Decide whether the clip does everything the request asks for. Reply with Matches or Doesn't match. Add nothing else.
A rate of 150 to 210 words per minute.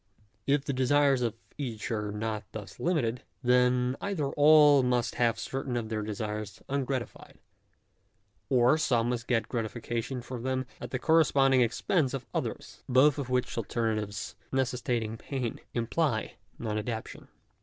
Doesn't match